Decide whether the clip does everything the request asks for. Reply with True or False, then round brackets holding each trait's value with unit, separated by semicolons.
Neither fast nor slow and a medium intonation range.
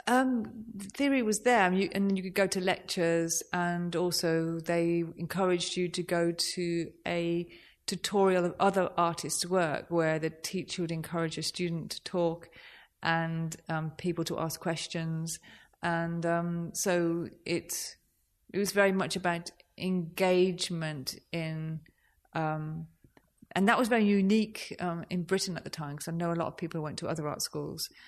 False (165 wpm; 2.2 semitones)